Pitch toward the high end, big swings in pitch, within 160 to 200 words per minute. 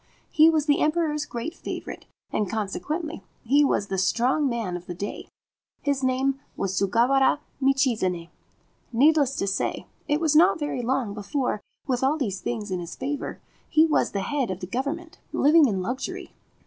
Yes: very high, 265 Hz; wide, 6.3 semitones; average, 170 wpm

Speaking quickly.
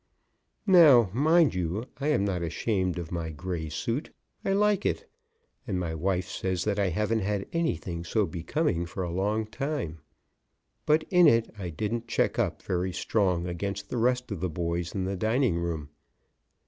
No: average, 175 wpm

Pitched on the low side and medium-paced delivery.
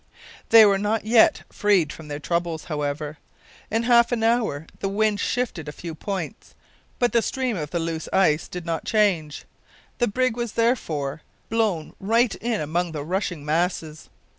No: high, 190 Hz; average, 165 wpm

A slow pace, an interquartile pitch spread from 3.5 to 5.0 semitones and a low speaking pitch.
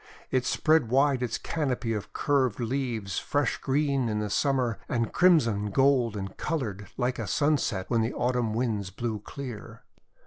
No: average, 150 wpm; average, 4.1 semitones; low, 125 Hz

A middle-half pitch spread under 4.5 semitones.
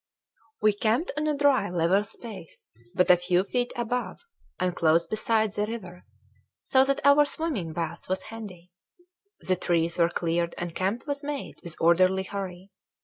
No: wide, 5.5 semitones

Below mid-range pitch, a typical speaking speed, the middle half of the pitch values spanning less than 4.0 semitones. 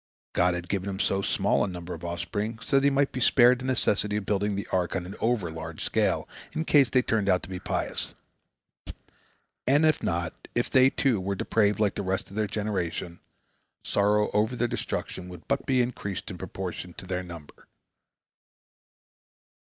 No: low, 100 Hz; average, 185 wpm; average, 4.9 semitones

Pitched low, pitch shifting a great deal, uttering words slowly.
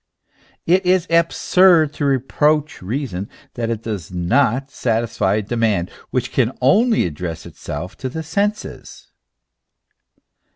Yes: low, 125 Hz; wide, 7.6 semitones; slow, 120 wpm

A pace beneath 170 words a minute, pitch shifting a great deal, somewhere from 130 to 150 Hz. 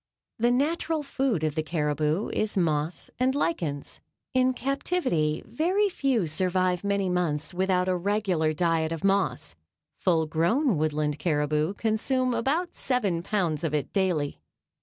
No: average, 140 wpm; wide, 7.9 semitones; medium, 185 Hz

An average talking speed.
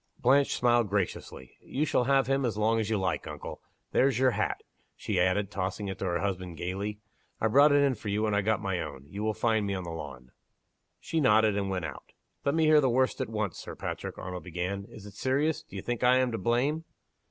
No: fast, 235 wpm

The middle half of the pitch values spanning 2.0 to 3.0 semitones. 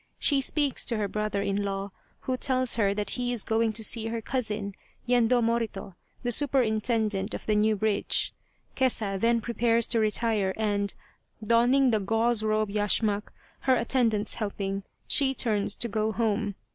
Yes: narrow, 2.4 semitones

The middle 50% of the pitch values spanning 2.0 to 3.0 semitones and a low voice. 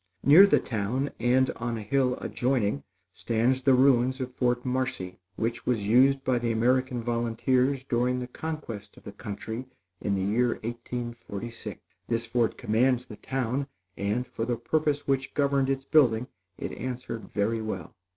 Yes: narrow, 2.5 semitones; low, 125 Hz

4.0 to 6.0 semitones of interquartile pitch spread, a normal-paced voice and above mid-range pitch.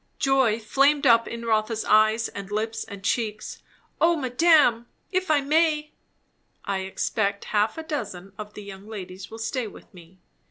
Yes: average, 5.1 semitones; average, 160 wpm; high, 225 Hz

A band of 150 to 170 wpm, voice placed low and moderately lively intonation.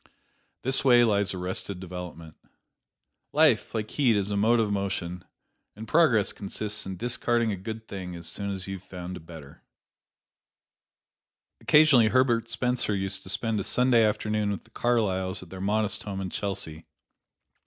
Yes: average, 160 wpm; low, 100 Hz; average, 3.3 semitones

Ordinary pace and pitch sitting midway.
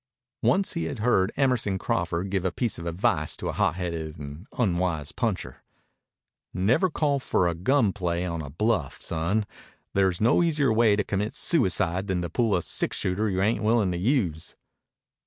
No: average, 175 wpm; very low, 95 Hz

